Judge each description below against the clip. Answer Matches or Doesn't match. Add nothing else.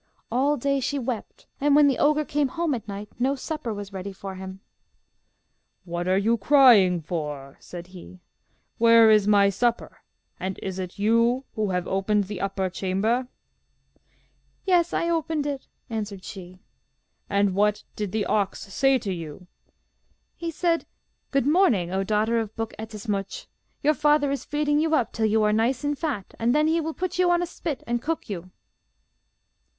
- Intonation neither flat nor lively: Doesn't match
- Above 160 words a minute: Matches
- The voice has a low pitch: Doesn't match